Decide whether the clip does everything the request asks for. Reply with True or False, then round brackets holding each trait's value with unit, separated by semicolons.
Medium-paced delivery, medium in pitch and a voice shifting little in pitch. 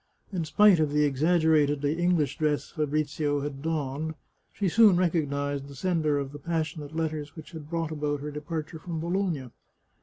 True (170 wpm; 155 Hz; 2.3 semitones)